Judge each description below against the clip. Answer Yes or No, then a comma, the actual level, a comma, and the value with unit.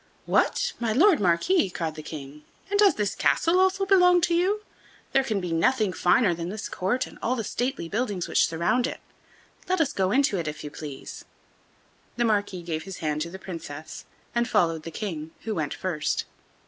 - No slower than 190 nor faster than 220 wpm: Yes, average, 195 wpm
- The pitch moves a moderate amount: No, wide, 7.8 semitones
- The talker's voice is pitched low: No, high, 195 Hz